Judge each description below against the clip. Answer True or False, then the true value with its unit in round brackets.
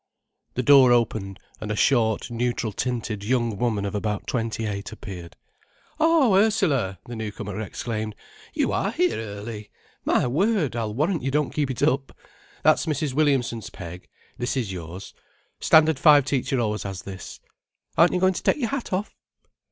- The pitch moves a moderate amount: False (5.7 semitones)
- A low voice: True (120 Hz)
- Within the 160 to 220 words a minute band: True (165 wpm)